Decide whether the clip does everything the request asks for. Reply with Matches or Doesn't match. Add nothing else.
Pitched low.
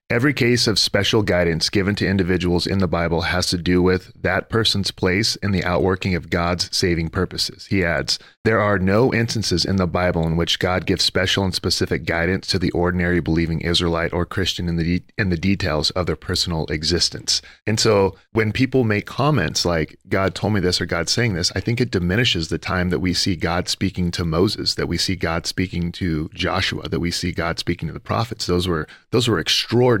Matches